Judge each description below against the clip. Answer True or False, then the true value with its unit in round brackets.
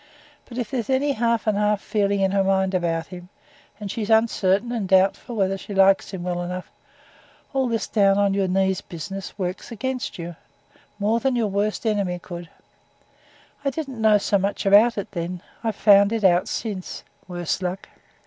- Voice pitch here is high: True (200 Hz)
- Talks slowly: False (185 wpm)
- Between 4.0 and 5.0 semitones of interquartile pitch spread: False (3.1 semitones)